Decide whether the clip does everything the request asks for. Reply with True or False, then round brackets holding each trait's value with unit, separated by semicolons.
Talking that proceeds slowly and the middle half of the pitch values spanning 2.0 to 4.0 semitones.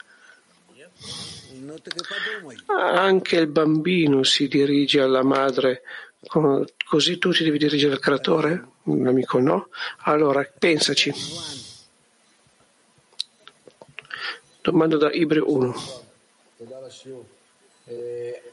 False (75 wpm; 4.8 semitones)